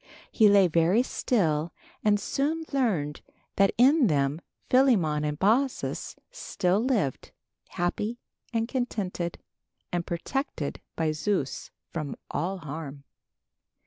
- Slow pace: Yes, slow, 110 wpm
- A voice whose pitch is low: No, high, 190 Hz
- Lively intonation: Yes, wide, 7.5 semitones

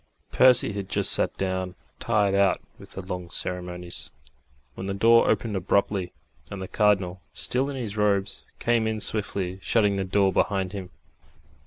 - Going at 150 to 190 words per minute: Yes, average, 160 wpm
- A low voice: Yes, low, 100 Hz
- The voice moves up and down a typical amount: No, narrow, 2.2 semitones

